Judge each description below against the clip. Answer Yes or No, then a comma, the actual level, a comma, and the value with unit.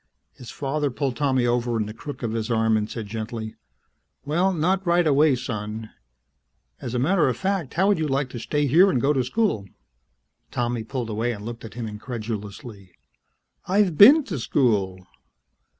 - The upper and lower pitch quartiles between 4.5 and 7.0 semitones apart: Yes, wide, 5.4 semitones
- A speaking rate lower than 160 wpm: No, average, 180 wpm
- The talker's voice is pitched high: No, low, 125 Hz